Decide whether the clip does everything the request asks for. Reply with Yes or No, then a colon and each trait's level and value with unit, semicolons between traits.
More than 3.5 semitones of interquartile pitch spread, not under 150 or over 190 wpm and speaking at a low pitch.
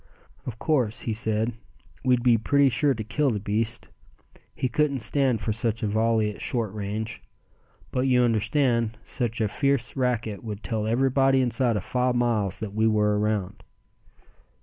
No: average, 2.9 semitones; average, 165 wpm; low, 115 Hz